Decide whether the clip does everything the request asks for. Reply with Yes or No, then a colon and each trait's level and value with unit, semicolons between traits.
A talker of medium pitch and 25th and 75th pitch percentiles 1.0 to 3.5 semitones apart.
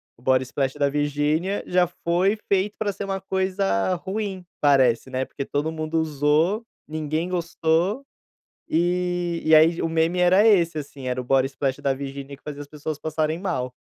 No: medium, 160 Hz; average, 4.2 semitones